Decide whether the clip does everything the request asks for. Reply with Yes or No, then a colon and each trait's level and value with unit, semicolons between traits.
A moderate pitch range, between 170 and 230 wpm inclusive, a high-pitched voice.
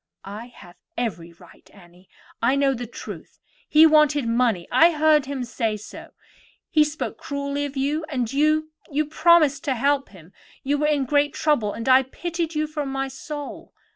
Yes: average, 4.2 semitones; average, 175 wpm; very high, 280 Hz